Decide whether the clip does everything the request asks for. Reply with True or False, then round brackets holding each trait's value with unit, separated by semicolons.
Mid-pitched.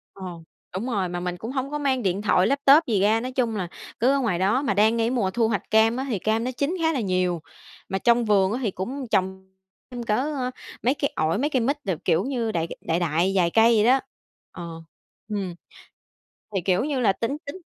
False (225 Hz)